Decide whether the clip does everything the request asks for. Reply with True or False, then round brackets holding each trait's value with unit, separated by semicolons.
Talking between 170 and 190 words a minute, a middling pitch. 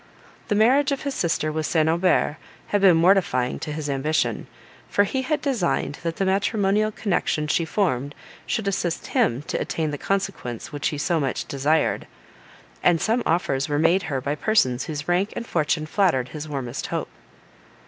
True (175 wpm; 165 Hz)